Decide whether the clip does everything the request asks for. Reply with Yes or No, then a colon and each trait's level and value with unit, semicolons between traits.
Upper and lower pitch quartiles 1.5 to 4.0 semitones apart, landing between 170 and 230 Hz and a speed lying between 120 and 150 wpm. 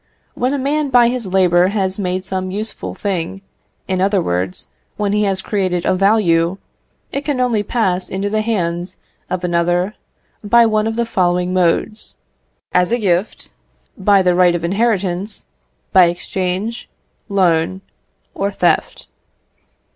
Yes: average, 3.1 semitones; high, 190 Hz; average, 145 wpm